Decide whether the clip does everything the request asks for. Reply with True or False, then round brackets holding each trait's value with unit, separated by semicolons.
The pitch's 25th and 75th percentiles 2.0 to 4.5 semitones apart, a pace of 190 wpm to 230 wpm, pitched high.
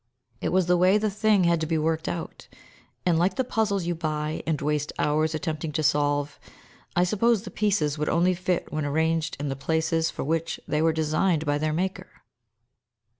False (3.1 semitones; 195 wpm; 160 Hz)